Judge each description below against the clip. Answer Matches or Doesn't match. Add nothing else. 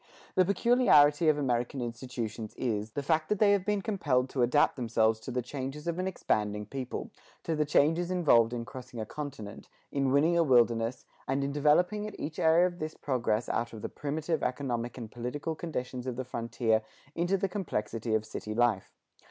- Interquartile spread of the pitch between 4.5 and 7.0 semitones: Matches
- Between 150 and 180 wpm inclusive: Doesn't match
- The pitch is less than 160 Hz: Matches